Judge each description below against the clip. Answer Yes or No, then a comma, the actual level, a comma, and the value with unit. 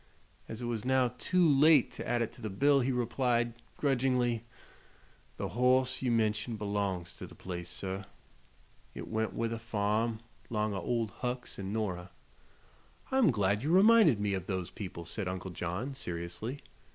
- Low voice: Yes, low, 115 Hz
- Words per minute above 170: No, average, 165 wpm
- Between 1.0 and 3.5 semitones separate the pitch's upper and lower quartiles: No, average, 4.2 semitones